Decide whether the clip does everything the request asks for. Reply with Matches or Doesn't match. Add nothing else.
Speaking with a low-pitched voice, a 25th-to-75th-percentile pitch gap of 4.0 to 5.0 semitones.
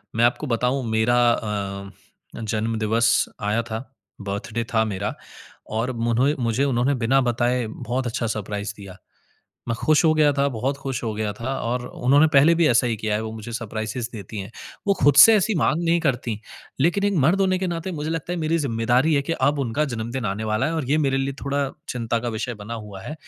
Matches